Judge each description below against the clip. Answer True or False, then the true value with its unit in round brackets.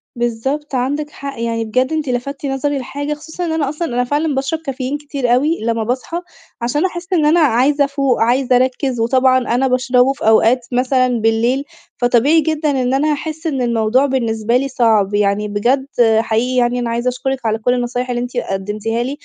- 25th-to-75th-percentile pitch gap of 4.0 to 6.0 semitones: False (3.2 semitones)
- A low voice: False (255 Hz)